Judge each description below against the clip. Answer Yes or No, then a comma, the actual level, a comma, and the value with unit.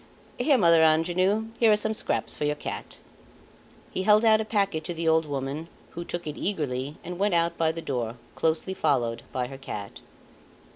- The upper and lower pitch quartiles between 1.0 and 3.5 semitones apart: No, average, 5.1 semitones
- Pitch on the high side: No, medium, 165 Hz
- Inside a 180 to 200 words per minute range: Yes, average, 190 wpm